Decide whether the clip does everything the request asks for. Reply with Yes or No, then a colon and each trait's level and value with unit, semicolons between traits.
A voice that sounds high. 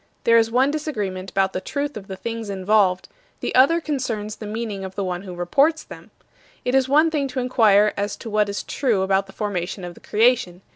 Yes: high, 210 Hz